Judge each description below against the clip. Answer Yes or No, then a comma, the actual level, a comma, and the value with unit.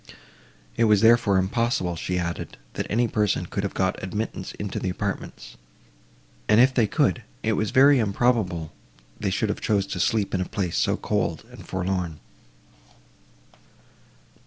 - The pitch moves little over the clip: No, average, 3.3 semitones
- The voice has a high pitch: No, low, 100 Hz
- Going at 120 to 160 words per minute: Yes, average, 150 wpm